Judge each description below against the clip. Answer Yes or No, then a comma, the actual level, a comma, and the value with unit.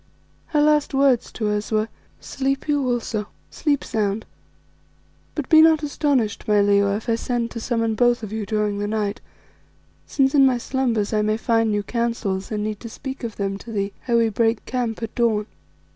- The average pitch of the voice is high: Yes, high, 225 Hz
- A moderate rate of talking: Yes, average, 190 wpm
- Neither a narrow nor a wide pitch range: Yes, average, 3.4 semitones